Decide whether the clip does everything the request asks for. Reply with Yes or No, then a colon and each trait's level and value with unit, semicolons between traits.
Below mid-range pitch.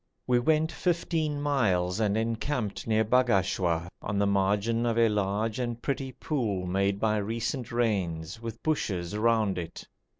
Yes: low, 110 Hz